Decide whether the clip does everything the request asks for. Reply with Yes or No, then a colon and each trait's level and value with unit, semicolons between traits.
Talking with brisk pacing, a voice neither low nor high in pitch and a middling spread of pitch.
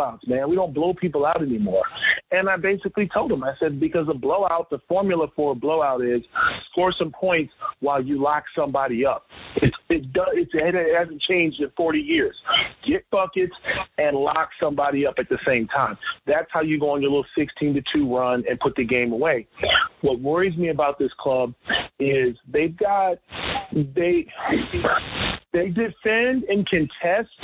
No: average, 175 wpm; medium, 160 Hz; average, 4.8 semitones